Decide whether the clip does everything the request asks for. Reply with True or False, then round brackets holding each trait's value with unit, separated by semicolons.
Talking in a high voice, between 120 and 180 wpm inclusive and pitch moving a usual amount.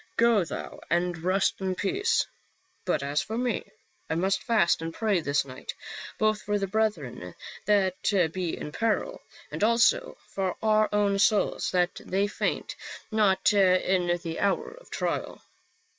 True (195 Hz; 150 wpm; 3.6 semitones)